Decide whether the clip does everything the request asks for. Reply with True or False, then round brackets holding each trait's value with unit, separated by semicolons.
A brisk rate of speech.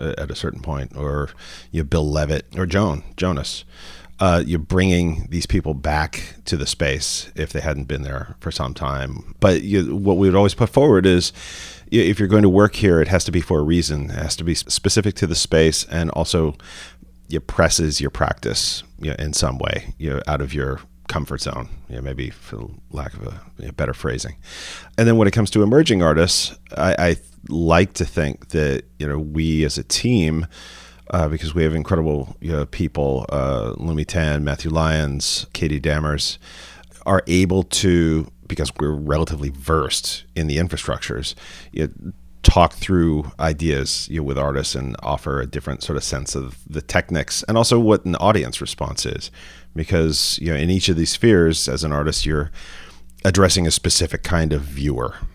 False (195 wpm)